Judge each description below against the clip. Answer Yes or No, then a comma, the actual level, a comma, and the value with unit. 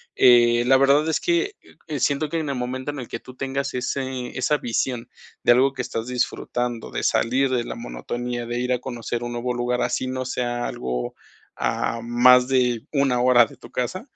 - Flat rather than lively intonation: Yes, narrow, 1.9 semitones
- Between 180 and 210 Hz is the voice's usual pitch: No, low, 125 Hz